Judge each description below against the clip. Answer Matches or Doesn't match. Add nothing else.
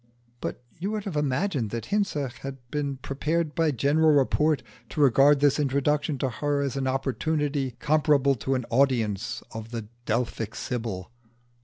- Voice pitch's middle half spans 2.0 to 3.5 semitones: Matches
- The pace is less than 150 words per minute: Doesn't match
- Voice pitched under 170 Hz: Matches